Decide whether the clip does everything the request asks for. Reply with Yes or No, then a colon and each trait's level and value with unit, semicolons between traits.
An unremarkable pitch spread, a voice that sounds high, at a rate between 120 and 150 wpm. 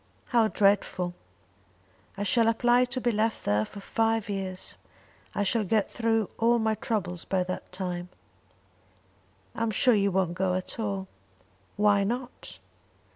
Yes: average, 3.3 semitones; high, 205 Hz; average, 145 wpm